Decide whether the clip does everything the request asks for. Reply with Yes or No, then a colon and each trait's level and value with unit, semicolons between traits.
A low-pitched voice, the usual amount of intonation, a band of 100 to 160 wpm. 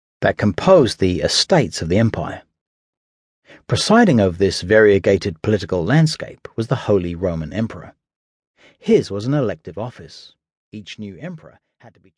Yes: low, 100 Hz; average, 4.1 semitones; average, 145 wpm